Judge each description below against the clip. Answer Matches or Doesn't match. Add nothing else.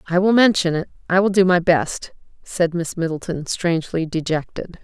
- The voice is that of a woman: Matches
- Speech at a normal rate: Matches